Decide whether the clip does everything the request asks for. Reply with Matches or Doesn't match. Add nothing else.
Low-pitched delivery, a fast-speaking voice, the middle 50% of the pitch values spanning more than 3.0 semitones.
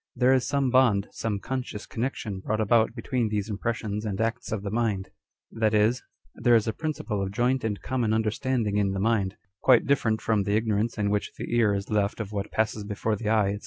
Doesn't match